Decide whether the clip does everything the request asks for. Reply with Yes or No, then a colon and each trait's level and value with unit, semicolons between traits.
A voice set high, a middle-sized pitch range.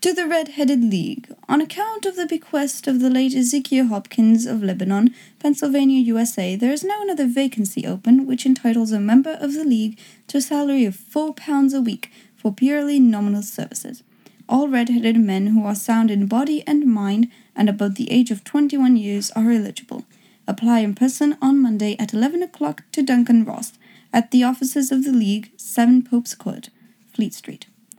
Yes: high, 245 Hz; average, 3.7 semitones